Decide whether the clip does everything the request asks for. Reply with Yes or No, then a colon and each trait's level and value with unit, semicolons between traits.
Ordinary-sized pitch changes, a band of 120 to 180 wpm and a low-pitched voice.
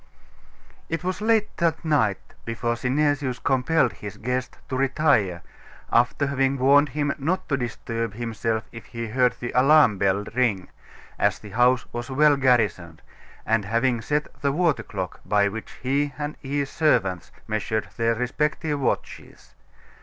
Yes: average, 4.3 semitones; average, 145 wpm; low, 125 Hz